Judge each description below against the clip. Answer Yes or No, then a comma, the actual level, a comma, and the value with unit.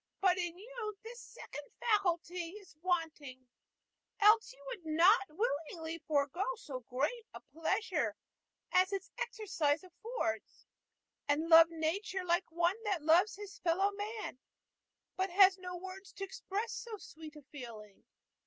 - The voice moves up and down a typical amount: Yes, average, 4.2 semitones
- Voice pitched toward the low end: No, very high, 360 Hz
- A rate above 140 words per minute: No, slow, 135 wpm